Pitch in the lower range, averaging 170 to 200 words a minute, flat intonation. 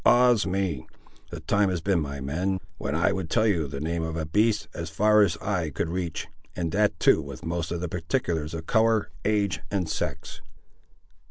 No: very low, 85 Hz; average, 195 wpm; average, 4.0 semitones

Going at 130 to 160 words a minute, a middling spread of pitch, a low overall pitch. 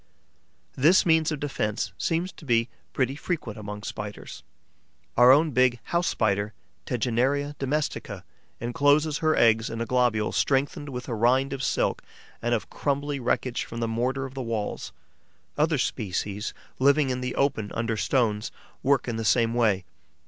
Yes: average, 155 wpm; average, 3.9 semitones; low, 125 Hz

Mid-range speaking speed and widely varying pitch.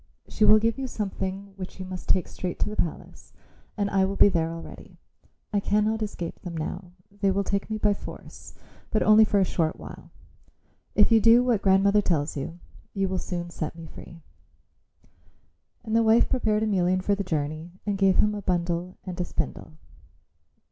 No: average, 190 wpm; average, 3.2 semitones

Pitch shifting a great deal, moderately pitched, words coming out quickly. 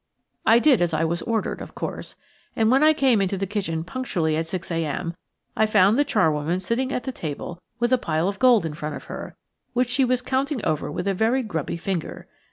No: wide, 7.0 semitones; high, 195 Hz; fast, 220 wpm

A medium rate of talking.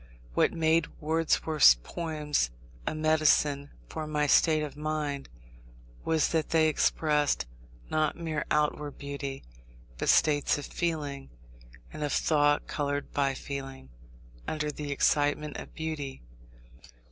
No: slow, 120 wpm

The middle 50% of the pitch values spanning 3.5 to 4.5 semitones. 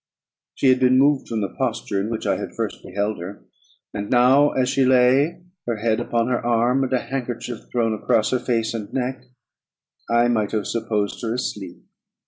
No: average, 2.8 semitones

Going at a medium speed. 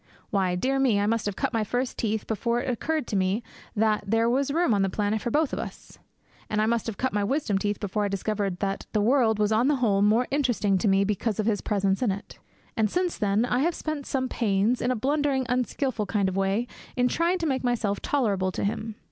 No: fast, 245 wpm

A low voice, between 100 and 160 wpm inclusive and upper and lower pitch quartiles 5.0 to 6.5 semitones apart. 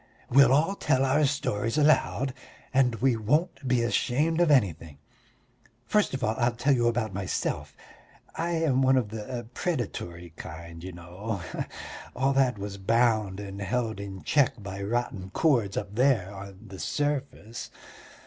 Yes: low, 120 Hz; average, 150 wpm; average, 5.3 semitones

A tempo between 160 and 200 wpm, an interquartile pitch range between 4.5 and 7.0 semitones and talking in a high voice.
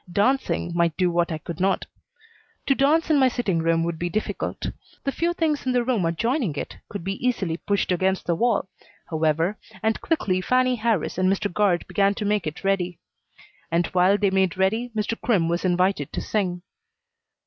Yes: average, 190 wpm; average, 5.0 semitones; high, 195 Hz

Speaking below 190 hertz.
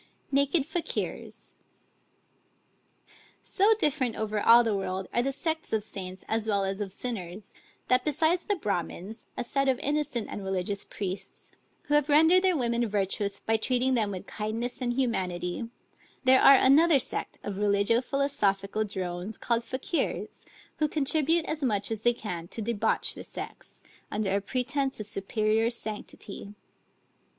No: high, 230 Hz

